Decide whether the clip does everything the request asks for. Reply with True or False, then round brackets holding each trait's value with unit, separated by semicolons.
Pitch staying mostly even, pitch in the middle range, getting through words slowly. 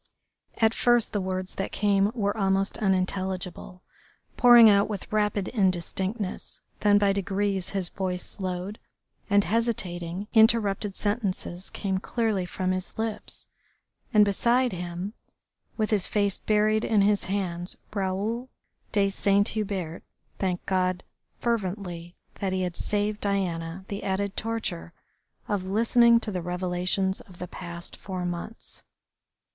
False (2.3 semitones; 195 Hz; 130 wpm)